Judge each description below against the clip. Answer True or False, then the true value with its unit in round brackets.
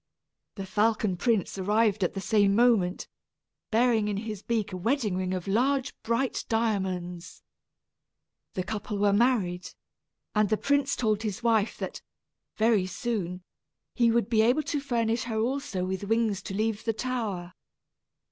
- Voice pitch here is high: True (215 Hz)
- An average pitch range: True (3.3 semitones)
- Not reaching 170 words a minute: True (150 wpm)